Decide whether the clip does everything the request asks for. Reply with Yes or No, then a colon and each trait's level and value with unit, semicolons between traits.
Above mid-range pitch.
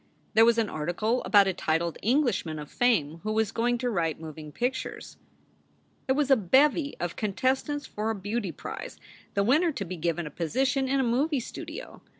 Yes: high, 220 Hz